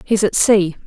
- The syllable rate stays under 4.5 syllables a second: Yes, 4.3 syllables/s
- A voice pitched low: No, high, 195 Hz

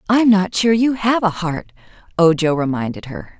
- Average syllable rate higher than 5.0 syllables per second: No, 4.7 syllables/s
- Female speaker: Yes, female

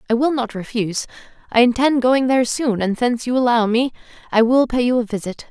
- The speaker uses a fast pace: Yes, fast, 220 wpm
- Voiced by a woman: Yes, female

